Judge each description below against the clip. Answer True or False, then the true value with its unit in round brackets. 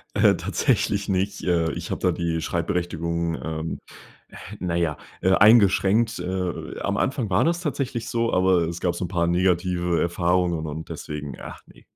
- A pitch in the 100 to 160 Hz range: False (90 Hz)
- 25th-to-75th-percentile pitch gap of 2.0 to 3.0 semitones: True (2.7 semitones)